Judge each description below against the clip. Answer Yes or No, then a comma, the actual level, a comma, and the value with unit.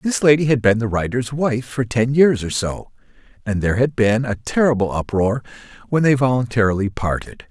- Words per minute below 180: No, average, 185 wpm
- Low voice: Yes, low, 120 Hz